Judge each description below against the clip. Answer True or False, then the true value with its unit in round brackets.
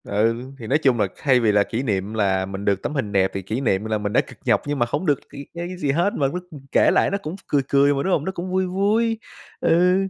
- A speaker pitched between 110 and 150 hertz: True (140 Hz)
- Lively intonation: True (8.6 semitones)